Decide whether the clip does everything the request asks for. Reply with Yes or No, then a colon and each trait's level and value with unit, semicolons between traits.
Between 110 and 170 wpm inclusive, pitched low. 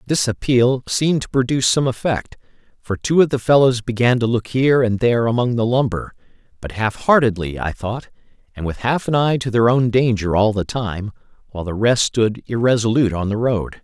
No: average, 200 wpm; low, 120 Hz